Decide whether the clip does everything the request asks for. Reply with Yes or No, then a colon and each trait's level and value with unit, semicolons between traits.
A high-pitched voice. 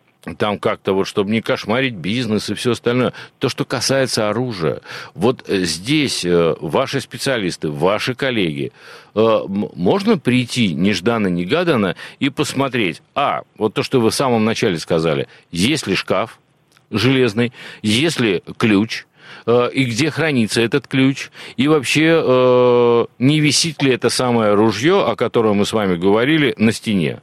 No: low, 125 Hz